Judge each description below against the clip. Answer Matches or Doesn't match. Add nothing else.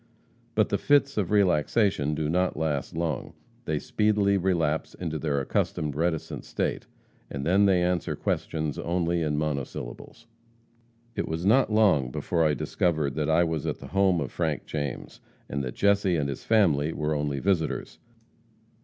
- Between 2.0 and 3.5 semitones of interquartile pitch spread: Doesn't match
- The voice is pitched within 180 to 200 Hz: Doesn't match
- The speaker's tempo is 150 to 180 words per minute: Matches